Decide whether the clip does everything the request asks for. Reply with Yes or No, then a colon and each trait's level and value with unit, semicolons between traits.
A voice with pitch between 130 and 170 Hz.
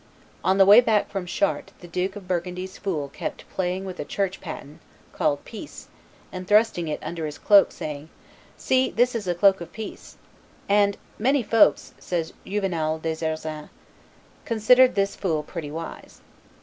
No: medium, 185 Hz